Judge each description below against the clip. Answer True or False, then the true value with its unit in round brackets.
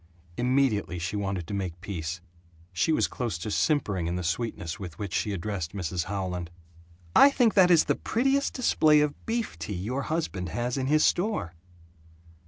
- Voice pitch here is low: True (105 Hz)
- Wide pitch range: True (9.0 semitones)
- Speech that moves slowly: False (175 wpm)